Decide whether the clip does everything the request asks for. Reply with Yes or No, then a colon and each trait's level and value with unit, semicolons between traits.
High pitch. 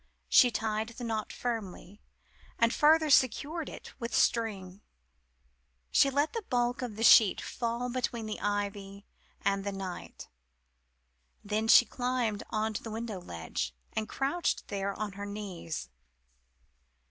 Yes: high, 220 Hz